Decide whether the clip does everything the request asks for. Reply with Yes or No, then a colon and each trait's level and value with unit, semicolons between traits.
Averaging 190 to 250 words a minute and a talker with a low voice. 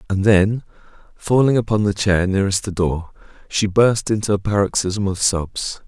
No: average, 165 wpm; low, 100 Hz